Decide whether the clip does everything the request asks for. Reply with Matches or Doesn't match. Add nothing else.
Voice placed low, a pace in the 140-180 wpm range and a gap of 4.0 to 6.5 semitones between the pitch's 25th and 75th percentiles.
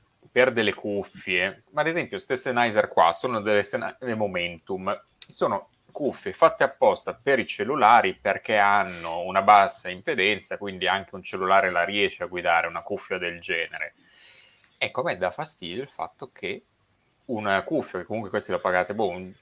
Matches